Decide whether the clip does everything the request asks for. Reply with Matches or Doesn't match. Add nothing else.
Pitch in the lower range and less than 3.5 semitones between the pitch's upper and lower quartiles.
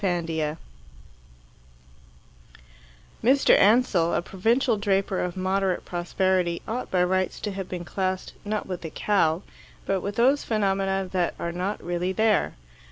Doesn't match